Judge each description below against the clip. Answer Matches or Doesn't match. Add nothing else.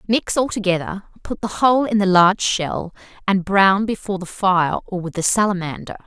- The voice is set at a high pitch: Matches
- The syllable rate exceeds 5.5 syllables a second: Doesn't match